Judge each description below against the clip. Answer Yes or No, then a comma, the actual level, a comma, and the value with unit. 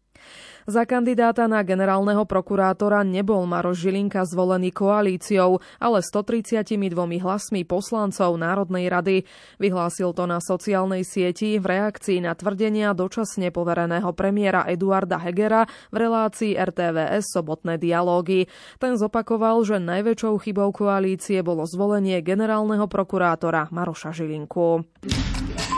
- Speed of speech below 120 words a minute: Yes, slow, 110 wpm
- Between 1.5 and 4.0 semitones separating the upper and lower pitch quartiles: Yes, average, 2.8 semitones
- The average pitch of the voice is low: No, high, 190 Hz